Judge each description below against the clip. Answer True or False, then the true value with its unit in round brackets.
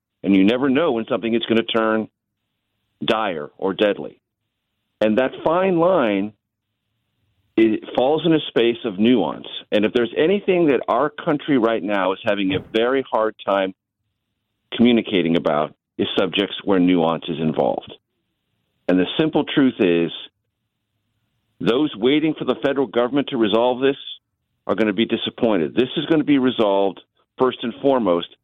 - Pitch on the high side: False (110 Hz)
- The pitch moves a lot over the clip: False (3.4 semitones)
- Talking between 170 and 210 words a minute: False (160 wpm)